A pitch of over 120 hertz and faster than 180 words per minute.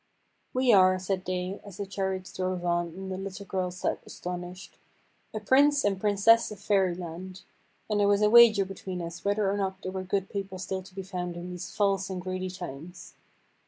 Yes: high, 190 Hz; average, 195 wpm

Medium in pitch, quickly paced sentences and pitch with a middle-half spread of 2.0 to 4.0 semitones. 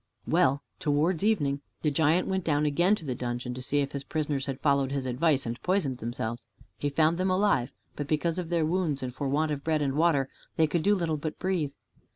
Yes: medium, 150 Hz; fast, 220 wpm; average, 3.5 semitones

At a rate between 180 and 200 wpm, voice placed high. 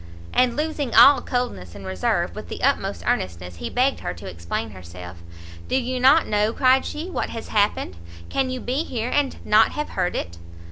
Yes: average, 190 wpm; high, 225 Hz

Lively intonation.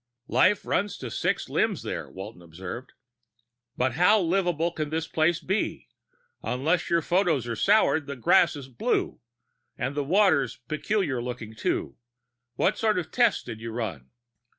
Yes: wide, 7.0 semitones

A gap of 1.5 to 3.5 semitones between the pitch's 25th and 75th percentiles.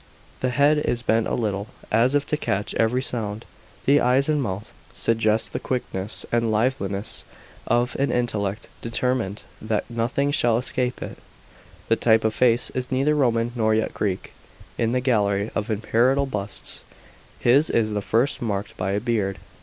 Yes: average, 3.1 semitones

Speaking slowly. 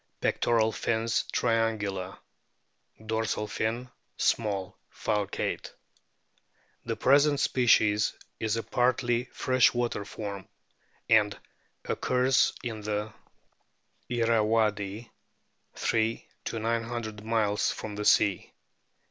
Yes: slow, 85 wpm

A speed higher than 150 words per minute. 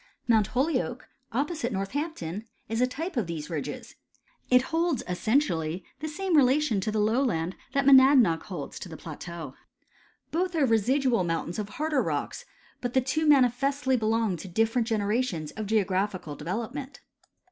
No: average, 145 wpm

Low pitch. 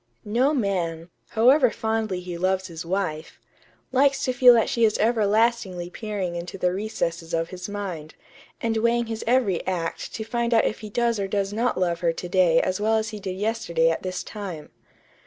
No: high, 200 Hz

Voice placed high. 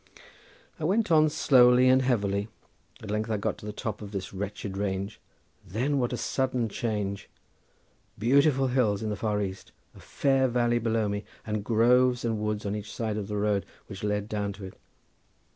No: low, 110 Hz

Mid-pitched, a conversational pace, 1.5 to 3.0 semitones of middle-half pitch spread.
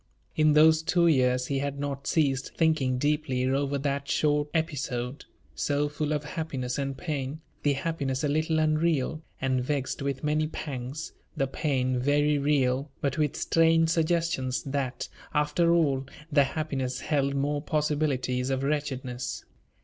Yes: medium, 145 Hz; average, 145 wpm; narrow, 2.5 semitones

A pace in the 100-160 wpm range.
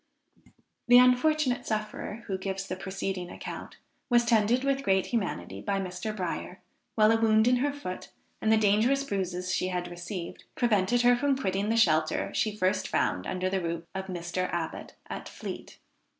No: average, 170 wpm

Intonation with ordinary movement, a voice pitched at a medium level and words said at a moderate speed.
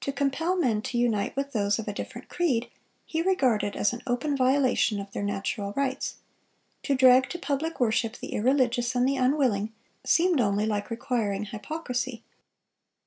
No: average, 4.6 semitones; very high, 250 Hz; average, 165 wpm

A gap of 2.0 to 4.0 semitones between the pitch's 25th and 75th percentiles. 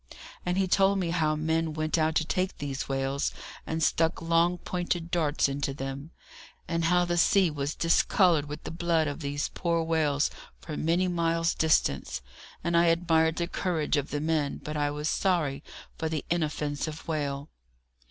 Yes: narrow, 2.6 semitones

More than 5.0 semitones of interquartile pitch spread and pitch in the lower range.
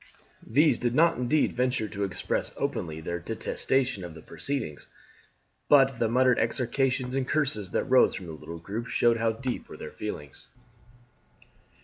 Yes: wide, 5.4 semitones; low, 120 Hz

